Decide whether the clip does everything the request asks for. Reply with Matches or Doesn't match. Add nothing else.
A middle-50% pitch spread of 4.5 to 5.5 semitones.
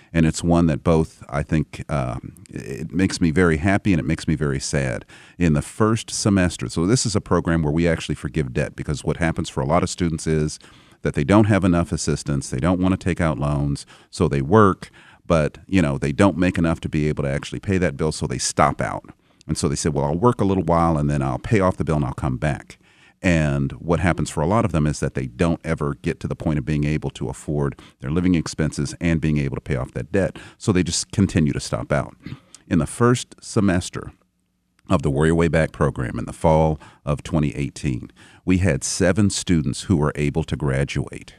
Doesn't match